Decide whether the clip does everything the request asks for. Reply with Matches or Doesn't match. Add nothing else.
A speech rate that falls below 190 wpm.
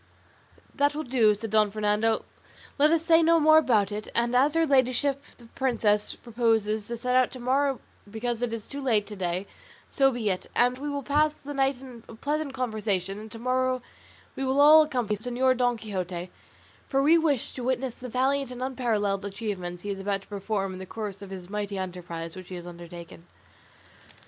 Doesn't match